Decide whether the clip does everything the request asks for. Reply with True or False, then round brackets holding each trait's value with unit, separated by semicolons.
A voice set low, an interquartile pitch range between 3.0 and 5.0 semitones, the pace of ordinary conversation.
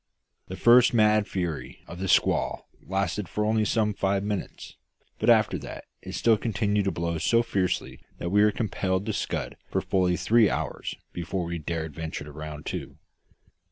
True (95 Hz; 3.7 semitones; 175 wpm)